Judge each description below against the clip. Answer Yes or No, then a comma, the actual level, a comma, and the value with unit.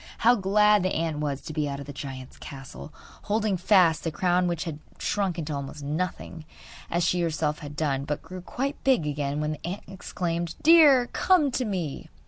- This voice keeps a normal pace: Yes, average, 195 wpm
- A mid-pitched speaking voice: Yes, medium, 170 Hz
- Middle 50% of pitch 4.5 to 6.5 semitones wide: Yes, average, 4.8 semitones